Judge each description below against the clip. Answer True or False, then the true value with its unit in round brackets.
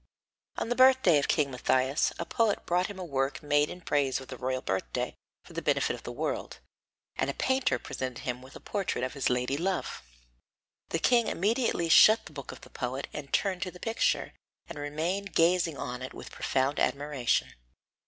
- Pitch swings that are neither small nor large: False (6.0 semitones)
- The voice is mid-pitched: True (150 Hz)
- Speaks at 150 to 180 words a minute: False (195 wpm)